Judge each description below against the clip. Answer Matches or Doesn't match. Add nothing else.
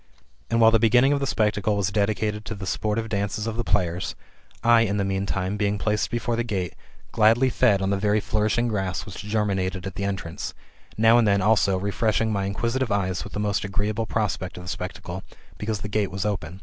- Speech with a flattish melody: Matches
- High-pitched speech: Doesn't match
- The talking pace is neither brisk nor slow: Doesn't match